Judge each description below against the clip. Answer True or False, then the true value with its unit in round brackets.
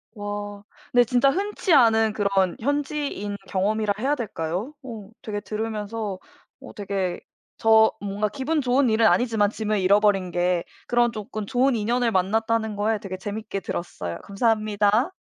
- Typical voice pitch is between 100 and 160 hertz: False (215 Hz)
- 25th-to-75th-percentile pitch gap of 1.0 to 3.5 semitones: True (2.8 semitones)